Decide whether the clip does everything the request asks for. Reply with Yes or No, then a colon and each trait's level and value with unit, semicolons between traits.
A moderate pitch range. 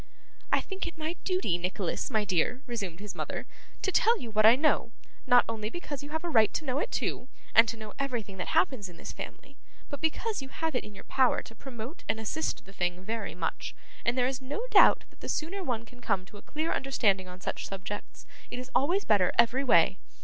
No: wide, 5.9 semitones